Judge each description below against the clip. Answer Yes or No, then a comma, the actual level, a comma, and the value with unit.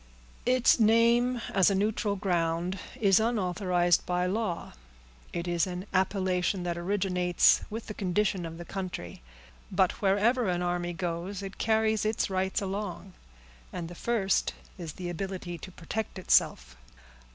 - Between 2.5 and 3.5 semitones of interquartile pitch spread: Yes, average, 3.0 semitones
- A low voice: No, high, 190 Hz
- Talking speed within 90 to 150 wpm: Yes, average, 140 wpm